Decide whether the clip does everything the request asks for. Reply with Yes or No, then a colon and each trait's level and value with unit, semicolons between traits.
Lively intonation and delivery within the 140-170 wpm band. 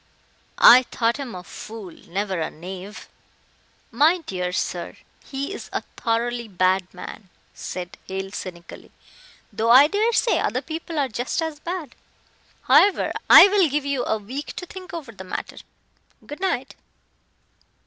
Yes: wide, 8.3 semitones; average, 145 wpm